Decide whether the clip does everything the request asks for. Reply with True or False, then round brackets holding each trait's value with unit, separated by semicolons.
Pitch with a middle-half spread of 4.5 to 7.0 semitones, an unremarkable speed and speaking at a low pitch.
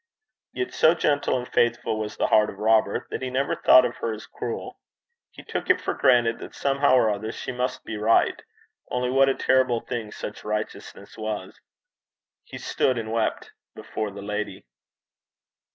False (3.1 semitones; 175 wpm; 115 Hz)